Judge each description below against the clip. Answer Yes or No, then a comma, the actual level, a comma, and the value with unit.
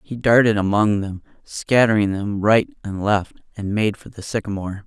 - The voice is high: No, low, 105 Hz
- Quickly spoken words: No, average, 175 wpm